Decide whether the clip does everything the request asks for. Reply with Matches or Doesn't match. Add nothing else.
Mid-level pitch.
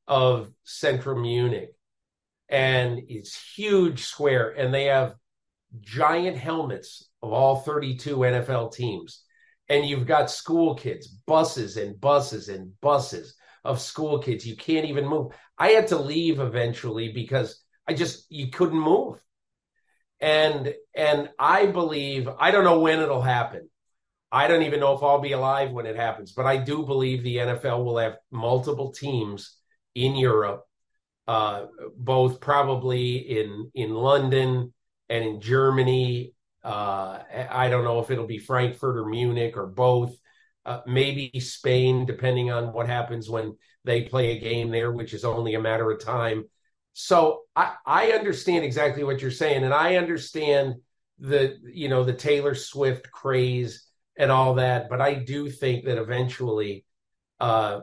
Doesn't match